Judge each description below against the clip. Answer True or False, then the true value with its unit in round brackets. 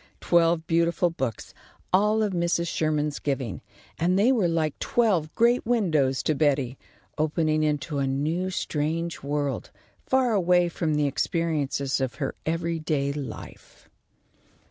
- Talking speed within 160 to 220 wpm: False (135 wpm)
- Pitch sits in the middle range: True (160 Hz)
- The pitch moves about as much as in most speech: True (3.2 semitones)